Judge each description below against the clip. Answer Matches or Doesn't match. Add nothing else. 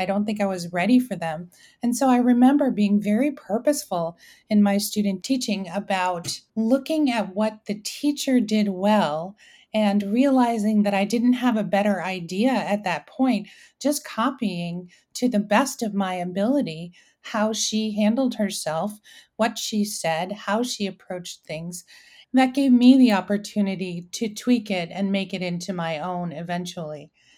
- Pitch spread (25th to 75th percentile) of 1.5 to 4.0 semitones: Doesn't match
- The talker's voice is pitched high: Matches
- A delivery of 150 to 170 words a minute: Matches